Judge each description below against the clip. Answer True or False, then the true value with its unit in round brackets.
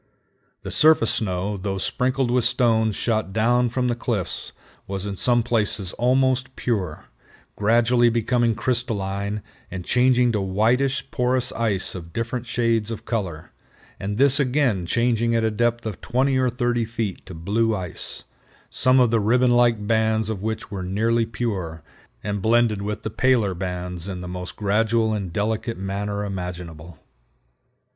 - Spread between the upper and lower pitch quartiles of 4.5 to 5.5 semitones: False (3.5 semitones)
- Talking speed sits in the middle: True (155 wpm)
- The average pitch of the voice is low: True (110 Hz)